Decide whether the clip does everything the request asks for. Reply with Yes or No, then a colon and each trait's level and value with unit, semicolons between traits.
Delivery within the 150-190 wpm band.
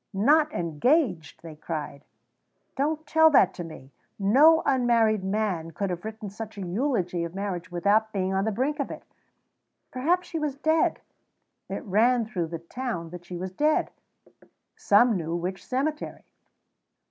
Yes: average, 155 wpm